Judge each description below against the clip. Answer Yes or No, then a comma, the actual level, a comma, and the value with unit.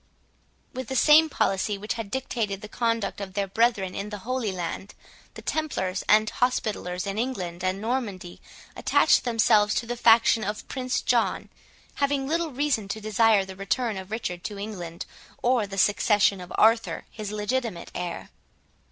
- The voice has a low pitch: No, high, 215 Hz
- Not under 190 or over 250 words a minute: No, average, 160 wpm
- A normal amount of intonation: Yes, average, 3.6 semitones